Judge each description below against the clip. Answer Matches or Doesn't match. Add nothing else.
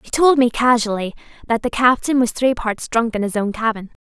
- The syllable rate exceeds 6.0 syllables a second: Doesn't match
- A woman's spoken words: Matches